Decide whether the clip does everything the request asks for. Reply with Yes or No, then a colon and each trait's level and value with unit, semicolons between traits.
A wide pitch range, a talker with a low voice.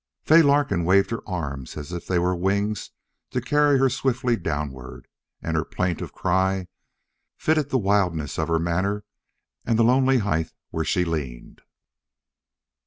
Yes: wide, 6.8 semitones; very low, 95 Hz